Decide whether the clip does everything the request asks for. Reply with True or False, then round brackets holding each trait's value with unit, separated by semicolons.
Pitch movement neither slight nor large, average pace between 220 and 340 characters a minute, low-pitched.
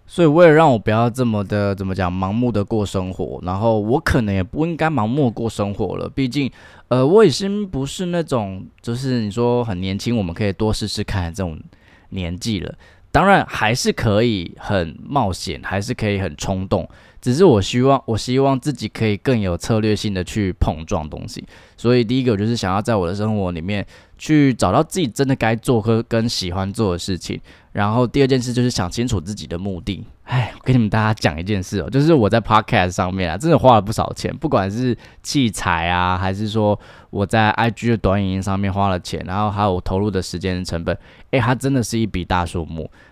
True (4.5 semitones; 320 characters per minute; 105 Hz)